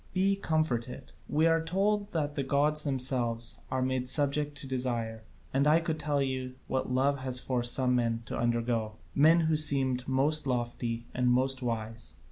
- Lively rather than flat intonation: No, average, 3.5 semitones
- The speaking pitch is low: Yes, low, 130 Hz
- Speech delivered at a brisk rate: No, average, 170 wpm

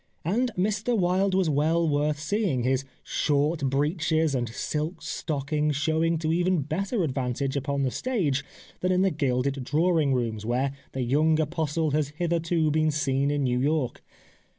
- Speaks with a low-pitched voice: No, medium, 150 Hz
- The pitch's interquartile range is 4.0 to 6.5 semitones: No, average, 3.5 semitones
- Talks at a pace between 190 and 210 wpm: No, average, 155 wpm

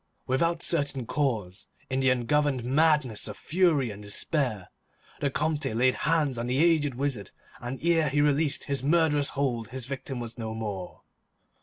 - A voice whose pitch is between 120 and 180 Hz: Yes, low, 135 Hz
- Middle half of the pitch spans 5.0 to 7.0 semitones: No, average, 3.9 semitones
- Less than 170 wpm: Yes, average, 160 wpm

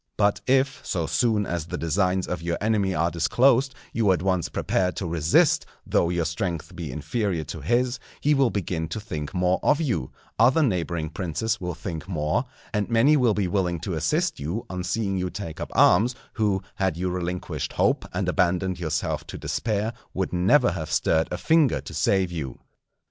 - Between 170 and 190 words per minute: Yes, average, 185 wpm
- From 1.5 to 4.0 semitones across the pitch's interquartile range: No, average, 4.7 semitones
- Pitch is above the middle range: No, very low, 95 Hz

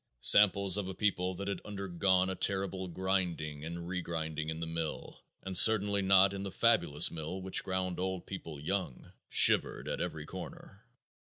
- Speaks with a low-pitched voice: Yes, very low, 95 Hz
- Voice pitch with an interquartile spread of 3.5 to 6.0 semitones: No, average, 2.8 semitones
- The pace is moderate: Yes, average, 165 wpm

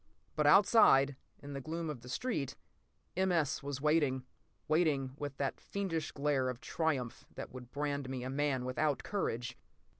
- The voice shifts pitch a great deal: No, average, 3.1 semitones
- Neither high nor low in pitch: Yes, medium, 145 Hz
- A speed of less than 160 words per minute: No, average, 170 wpm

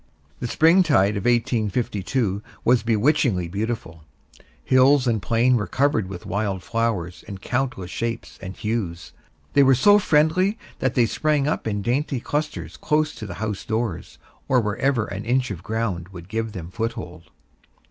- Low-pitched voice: Yes, low, 115 Hz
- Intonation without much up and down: No, average, 5.0 semitones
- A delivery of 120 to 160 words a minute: Yes, average, 155 wpm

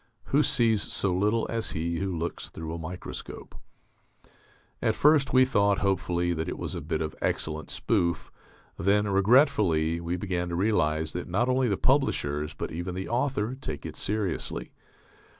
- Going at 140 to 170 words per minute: Yes, average, 165 wpm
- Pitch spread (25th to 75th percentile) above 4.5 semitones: Yes, average, 5.1 semitones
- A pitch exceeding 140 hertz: No, very low, 95 Hz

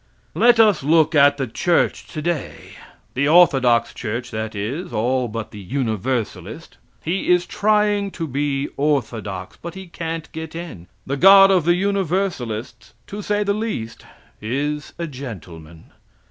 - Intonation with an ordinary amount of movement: No, wide, 7.2 semitones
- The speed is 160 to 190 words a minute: No, average, 145 wpm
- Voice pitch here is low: No, medium, 145 Hz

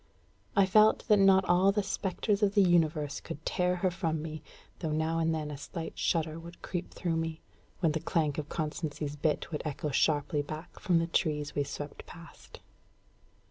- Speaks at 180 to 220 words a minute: Yes, average, 185 wpm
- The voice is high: No, medium, 165 Hz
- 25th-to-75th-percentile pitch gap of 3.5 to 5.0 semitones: No, average, 2.9 semitones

